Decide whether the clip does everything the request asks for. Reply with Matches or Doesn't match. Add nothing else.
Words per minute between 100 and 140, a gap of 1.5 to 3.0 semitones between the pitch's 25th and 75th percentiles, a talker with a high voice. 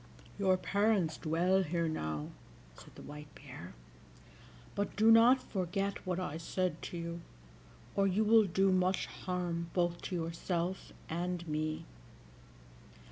Doesn't match